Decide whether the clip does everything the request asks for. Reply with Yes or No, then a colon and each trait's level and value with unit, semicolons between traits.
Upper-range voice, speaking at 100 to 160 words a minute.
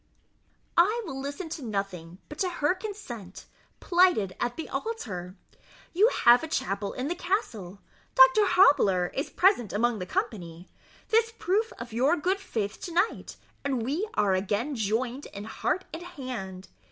Yes: very high, 260 Hz; average, 155 wpm